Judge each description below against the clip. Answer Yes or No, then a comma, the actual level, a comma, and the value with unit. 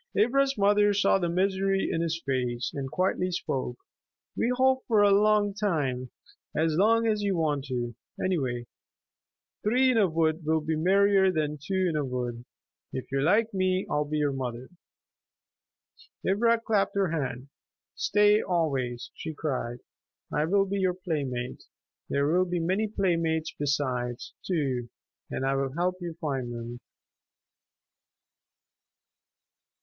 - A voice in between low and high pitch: Yes, medium, 165 Hz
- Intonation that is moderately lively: No, wide, 6.4 semitones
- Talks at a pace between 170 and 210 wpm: No, average, 145 wpm